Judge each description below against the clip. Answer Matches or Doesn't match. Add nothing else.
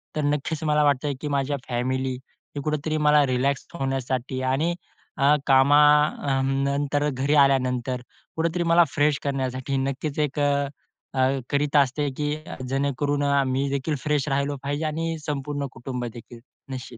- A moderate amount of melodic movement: Doesn't match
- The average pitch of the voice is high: Doesn't match